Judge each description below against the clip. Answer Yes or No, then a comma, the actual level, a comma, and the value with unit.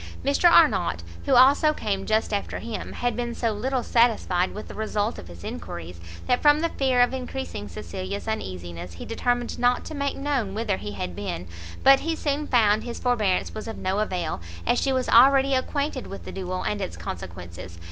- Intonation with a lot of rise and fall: Yes, wide, 6.6 semitones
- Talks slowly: No, average, 195 wpm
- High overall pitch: Yes, high, 220 Hz